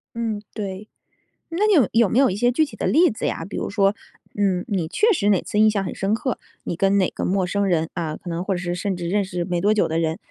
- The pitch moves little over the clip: No, average, 3.4 semitones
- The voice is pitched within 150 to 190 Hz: No, high, 200 Hz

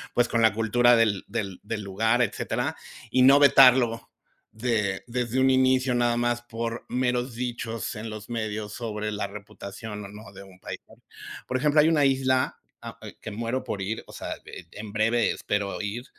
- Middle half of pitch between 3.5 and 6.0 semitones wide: No, average, 2.9 semitones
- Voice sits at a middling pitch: No, low, 115 Hz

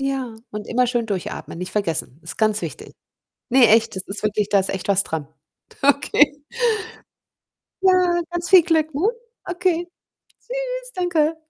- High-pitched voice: Yes, very high, 270 Hz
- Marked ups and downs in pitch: Yes, wide, 8.8 semitones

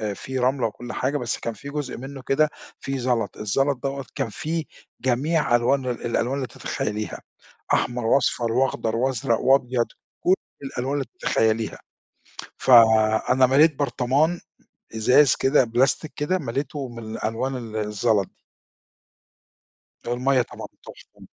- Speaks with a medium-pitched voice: No, low, 125 Hz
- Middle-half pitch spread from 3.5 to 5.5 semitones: No, average, 2.9 semitones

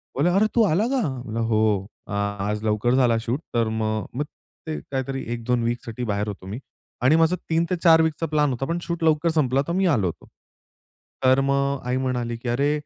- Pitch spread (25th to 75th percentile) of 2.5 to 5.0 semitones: No, wide, 5.6 semitones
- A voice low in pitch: Yes, low, 130 Hz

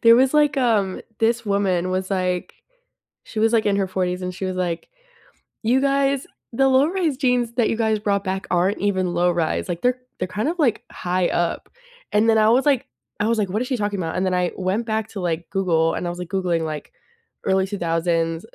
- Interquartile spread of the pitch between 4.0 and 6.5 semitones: Yes, average, 4.4 semitones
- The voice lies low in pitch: No, high, 200 Hz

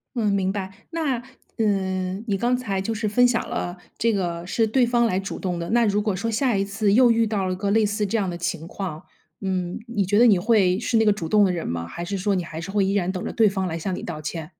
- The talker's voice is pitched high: Yes, high, 200 Hz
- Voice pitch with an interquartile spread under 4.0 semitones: Yes, average, 3.3 semitones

